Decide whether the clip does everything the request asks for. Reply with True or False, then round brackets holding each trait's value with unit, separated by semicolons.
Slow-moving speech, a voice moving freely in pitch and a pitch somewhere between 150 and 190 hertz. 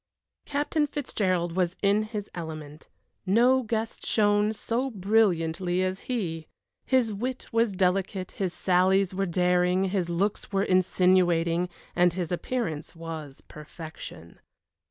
False (120 wpm; 3.7 semitones; 185 Hz)